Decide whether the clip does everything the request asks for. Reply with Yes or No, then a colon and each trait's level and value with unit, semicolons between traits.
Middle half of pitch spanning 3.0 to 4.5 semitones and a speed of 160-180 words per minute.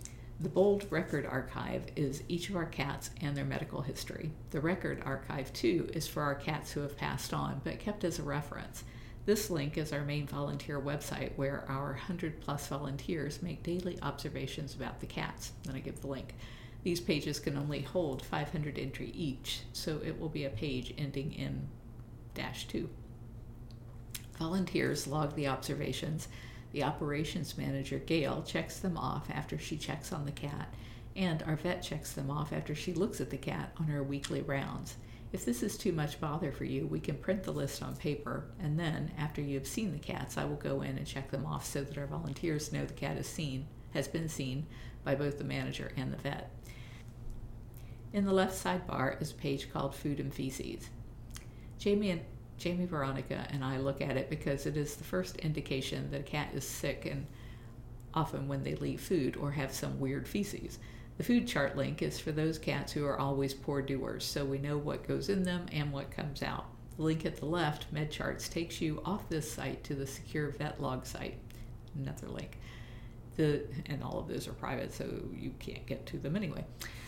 No: average, 4.2 semitones; average, 195 wpm